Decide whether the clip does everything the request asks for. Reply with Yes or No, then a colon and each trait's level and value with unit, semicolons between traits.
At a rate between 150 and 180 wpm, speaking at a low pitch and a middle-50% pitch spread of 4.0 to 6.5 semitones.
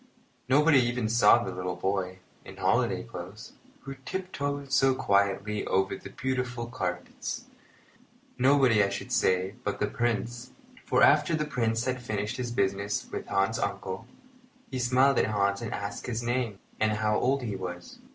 Yes: average, 160 wpm; low, 115 Hz; average, 4.4 semitones